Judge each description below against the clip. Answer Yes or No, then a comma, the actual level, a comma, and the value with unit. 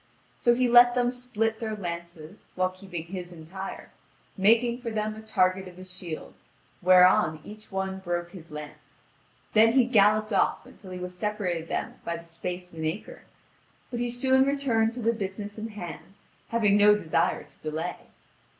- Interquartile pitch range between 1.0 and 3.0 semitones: No, average, 4.1 semitones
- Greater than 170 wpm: Yes, average, 180 wpm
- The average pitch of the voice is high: Yes, high, 195 Hz